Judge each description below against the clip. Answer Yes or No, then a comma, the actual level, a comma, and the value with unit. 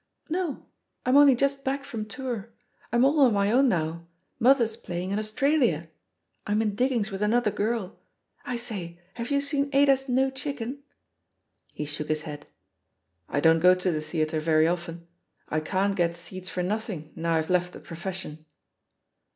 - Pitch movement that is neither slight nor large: No, wide, 7.4 semitones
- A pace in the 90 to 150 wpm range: No, average, 170 wpm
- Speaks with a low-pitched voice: No, high, 205 Hz